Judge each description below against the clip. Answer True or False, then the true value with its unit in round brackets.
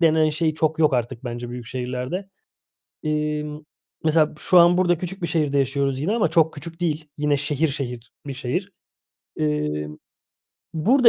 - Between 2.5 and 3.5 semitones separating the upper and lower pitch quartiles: False (4.2 semitones)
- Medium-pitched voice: True (150 Hz)